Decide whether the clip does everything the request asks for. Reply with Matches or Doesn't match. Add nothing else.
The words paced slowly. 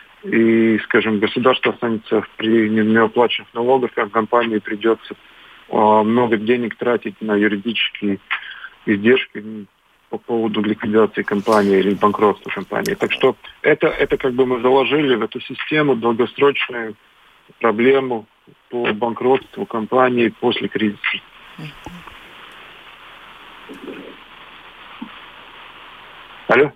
Matches